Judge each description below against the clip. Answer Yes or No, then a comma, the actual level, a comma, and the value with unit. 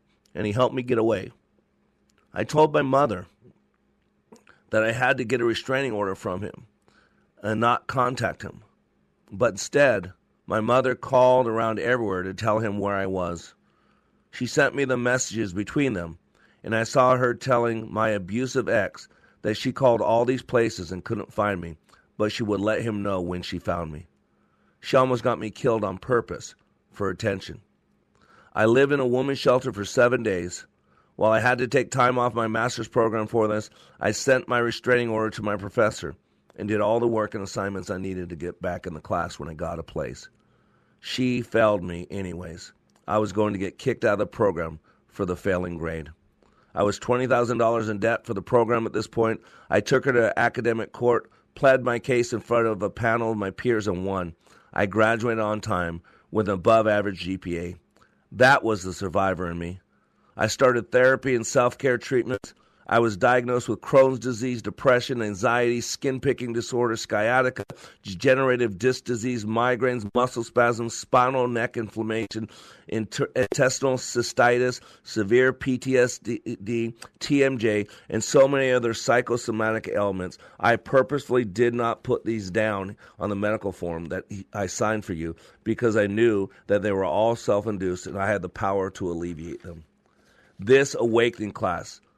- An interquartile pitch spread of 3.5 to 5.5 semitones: Yes, average, 4.1 semitones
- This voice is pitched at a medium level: No, low, 110 Hz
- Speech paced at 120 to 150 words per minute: No, average, 175 wpm